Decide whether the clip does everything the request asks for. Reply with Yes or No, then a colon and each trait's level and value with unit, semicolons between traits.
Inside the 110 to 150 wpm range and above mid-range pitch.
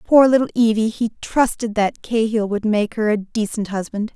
No: average, 190 wpm; high, 220 Hz